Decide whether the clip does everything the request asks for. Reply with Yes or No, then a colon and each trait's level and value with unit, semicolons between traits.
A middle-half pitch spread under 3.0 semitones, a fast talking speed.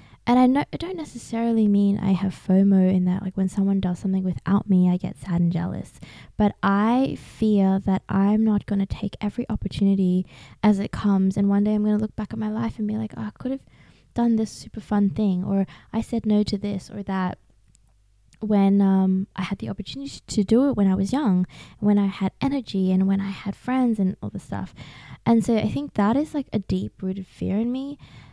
Yes: narrow, 2.4 semitones; fast, 230 wpm